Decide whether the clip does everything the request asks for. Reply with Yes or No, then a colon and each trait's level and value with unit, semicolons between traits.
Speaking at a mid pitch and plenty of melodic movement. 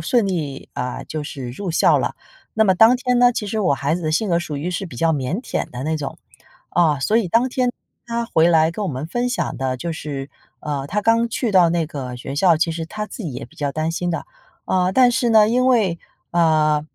Yes: medium, 170 Hz; wide, 6.4 semitones